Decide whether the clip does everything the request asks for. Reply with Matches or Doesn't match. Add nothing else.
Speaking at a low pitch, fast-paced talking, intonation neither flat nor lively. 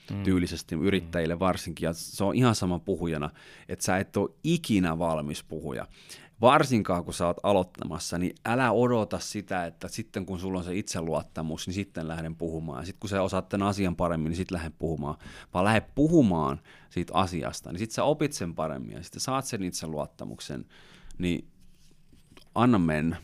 Matches